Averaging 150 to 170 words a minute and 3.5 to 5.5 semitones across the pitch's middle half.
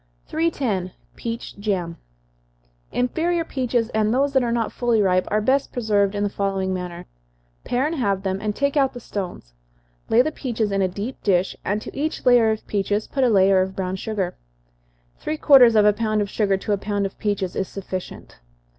No: average, 200 wpm; average, 4.1 semitones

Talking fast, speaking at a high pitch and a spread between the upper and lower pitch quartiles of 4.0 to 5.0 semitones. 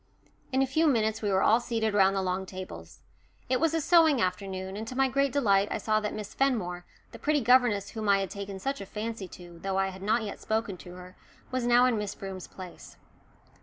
Yes: fast, 230 wpm; high, 210 Hz; average, 4.5 semitones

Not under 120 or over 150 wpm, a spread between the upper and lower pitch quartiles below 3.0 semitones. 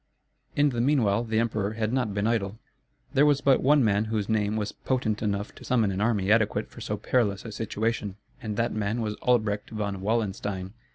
No: average, 195 wpm; narrow, 2.4 semitones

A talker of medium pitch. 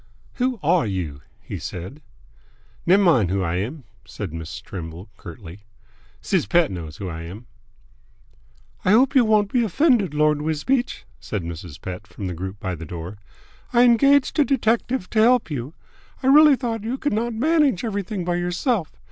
Yes: medium, 170 Hz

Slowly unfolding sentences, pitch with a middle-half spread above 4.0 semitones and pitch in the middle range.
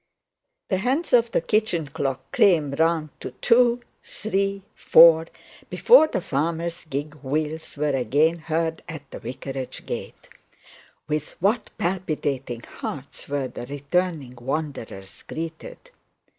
Yes: slow, 120 wpm; average, 4.8 semitones; medium, 160 Hz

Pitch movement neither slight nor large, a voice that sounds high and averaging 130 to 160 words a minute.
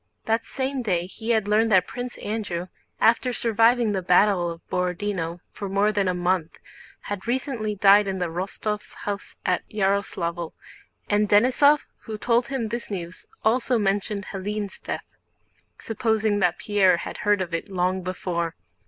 Yes: average, 3.3 semitones; high, 205 Hz; average, 155 wpm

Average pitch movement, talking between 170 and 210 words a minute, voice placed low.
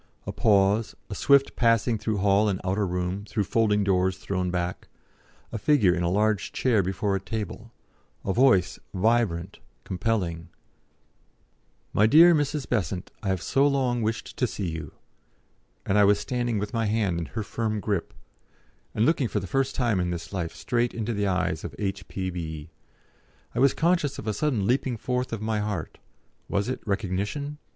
Yes: average, 4.1 semitones; average, 175 wpm; low, 105 Hz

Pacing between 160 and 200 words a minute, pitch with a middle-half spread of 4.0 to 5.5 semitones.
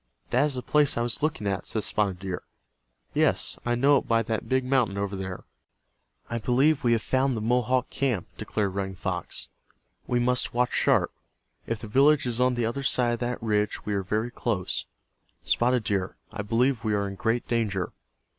No: average, 195 wpm; average, 3.6 semitones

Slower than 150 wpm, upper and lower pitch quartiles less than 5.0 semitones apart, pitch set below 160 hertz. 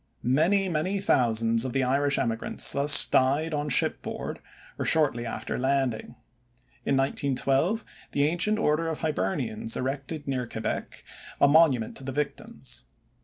Yes: average, 140 wpm; average, 3.7 semitones; medium, 140 Hz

